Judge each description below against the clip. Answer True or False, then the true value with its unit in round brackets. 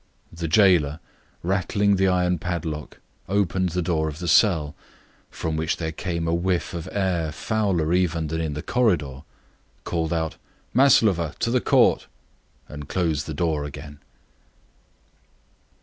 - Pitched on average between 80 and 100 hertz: True (85 Hz)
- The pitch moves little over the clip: False (3.0 semitones)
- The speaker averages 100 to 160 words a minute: True (150 wpm)